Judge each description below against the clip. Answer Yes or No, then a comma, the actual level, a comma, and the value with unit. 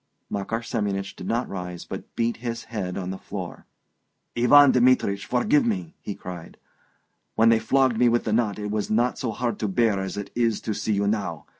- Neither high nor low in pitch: No, low, 110 Hz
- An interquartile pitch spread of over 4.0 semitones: No, average, 3.3 semitones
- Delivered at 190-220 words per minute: Yes, average, 200 wpm